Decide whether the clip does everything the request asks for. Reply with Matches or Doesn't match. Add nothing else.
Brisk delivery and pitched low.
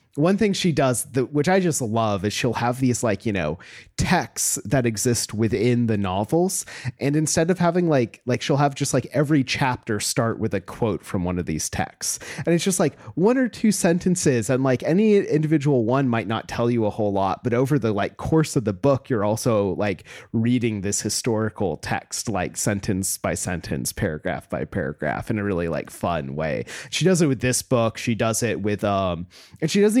Matches